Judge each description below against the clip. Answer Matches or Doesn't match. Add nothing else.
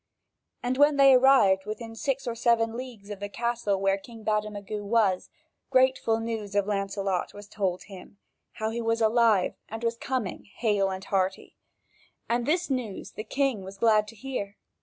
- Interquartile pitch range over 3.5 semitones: Doesn't match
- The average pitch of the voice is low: Doesn't match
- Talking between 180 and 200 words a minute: Doesn't match